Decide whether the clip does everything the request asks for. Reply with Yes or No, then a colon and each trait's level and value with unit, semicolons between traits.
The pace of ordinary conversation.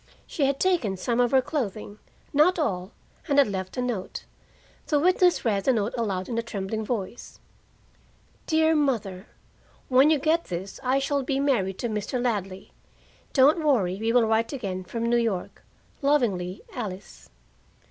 Yes: average, 155 wpm